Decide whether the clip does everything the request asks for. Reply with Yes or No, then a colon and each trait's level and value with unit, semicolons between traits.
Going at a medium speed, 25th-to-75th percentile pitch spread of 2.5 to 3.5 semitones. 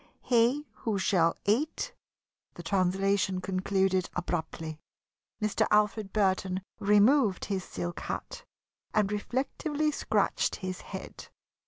No: slow, 110 wpm; average, 3.0 semitones